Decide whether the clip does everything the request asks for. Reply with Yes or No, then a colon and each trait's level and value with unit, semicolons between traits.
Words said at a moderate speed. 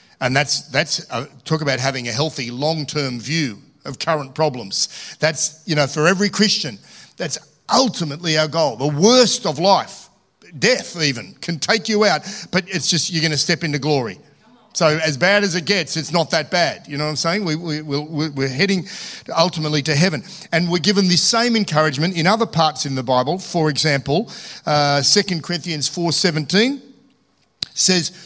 Yes: average, 180 wpm